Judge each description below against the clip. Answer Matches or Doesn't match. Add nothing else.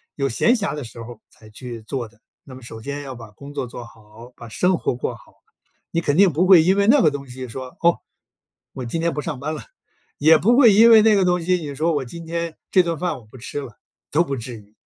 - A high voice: Doesn't match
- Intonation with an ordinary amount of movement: Doesn't match